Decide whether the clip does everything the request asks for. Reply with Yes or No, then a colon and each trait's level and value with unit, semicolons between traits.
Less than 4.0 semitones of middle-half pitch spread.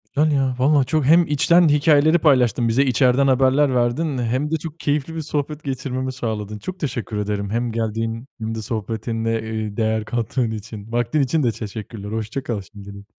No: average, 4.4 semitones